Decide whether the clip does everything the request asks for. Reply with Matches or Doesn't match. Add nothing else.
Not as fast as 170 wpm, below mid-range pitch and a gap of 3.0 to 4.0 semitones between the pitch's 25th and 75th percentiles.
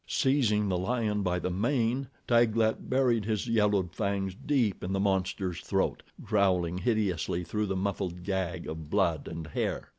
Matches